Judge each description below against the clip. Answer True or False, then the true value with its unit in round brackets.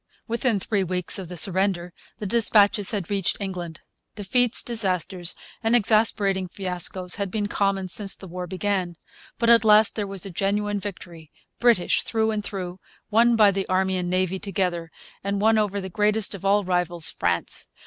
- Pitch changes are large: False (2.5 semitones)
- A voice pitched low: False (195 Hz)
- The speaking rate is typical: True (170 wpm)